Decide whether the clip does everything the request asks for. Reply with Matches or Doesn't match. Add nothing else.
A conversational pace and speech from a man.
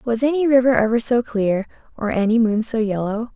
Doesn't match